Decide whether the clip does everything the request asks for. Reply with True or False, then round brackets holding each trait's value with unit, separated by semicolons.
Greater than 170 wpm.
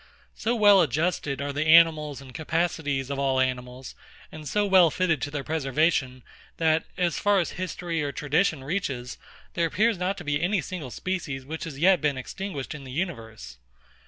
True (180 wpm)